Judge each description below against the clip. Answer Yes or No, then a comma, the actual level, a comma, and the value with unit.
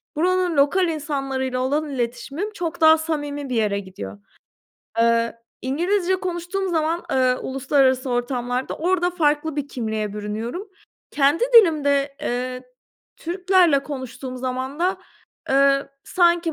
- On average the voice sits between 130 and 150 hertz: No, very high, 280 Hz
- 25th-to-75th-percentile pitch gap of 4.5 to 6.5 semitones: Yes, average, 5.2 semitones